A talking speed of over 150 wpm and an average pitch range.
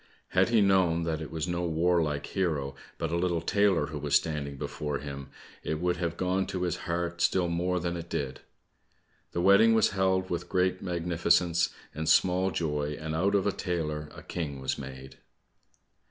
Yes: average, 185 wpm; average, 3.0 semitones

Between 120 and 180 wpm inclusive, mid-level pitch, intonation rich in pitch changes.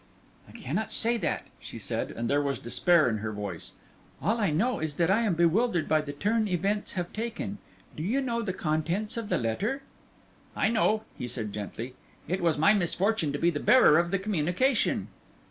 No: average, 195 wpm; medium, 175 Hz; wide, 6.5 semitones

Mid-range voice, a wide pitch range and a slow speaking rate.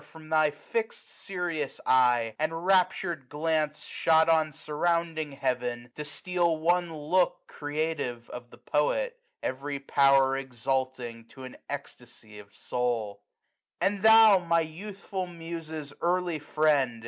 No: medium, 155 Hz; average, 4.4 semitones; slow, 125 wpm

